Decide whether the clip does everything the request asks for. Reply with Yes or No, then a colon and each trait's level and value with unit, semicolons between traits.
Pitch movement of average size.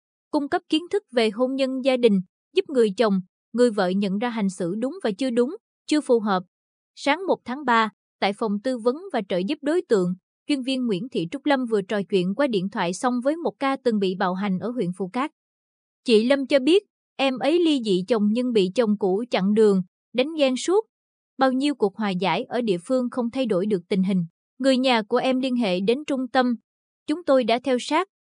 Yes: average, 4.9 semitones